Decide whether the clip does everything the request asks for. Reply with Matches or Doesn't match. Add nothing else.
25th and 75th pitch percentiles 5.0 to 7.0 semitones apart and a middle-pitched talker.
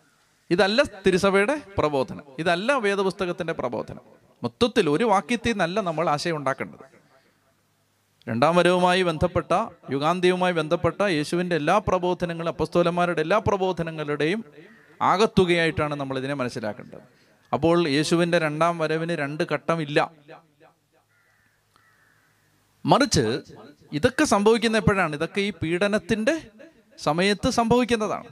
Doesn't match